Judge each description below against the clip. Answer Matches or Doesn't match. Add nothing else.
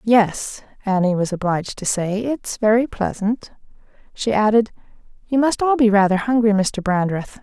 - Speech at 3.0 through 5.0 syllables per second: Matches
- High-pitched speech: Matches